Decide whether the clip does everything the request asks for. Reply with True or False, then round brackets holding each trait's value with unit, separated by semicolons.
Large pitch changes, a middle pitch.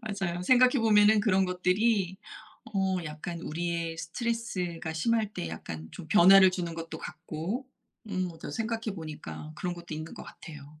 False (4.4 semitones; 180 Hz)